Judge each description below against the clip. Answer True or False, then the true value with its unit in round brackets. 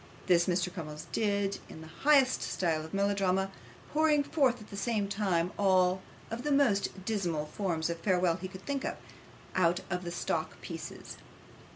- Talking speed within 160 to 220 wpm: True (165 wpm)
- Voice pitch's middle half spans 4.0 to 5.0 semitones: False (3.5 semitones)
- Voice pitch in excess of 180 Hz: True (190 Hz)